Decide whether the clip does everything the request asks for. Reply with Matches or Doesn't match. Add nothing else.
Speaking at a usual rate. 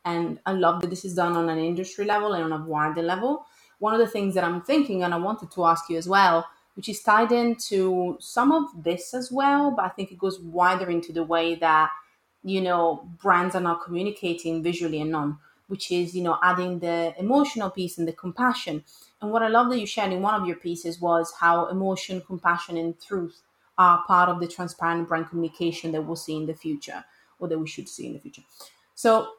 Doesn't match